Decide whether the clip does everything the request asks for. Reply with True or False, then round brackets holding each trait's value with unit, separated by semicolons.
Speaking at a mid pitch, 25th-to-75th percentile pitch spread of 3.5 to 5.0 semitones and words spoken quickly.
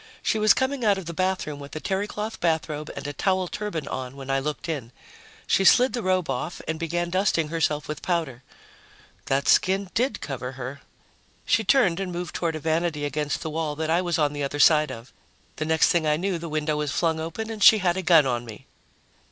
True (160 Hz; 4.0 semitones; 220 wpm)